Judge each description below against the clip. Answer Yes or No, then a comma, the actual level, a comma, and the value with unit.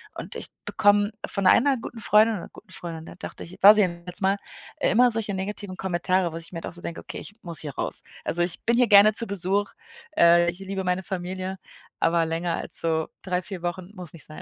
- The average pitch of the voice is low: No, medium, 185 Hz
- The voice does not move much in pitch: No, average, 3.0 semitones